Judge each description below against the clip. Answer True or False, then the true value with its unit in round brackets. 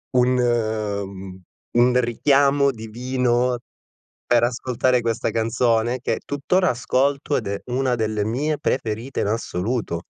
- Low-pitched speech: True (120 Hz)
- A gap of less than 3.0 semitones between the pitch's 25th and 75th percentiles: True (2.5 semitones)